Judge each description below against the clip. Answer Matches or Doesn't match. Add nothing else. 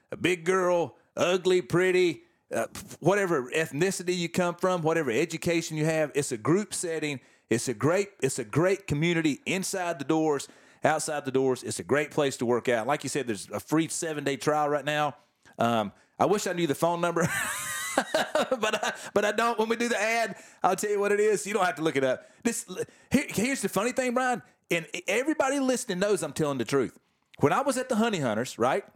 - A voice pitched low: Doesn't match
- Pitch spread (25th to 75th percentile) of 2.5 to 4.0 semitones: Doesn't match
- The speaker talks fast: Matches